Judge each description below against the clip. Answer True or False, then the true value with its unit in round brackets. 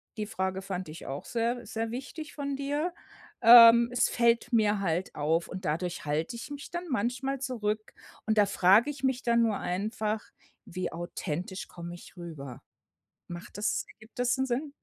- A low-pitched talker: False (220 Hz)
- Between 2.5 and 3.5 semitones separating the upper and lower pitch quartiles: False (5.3 semitones)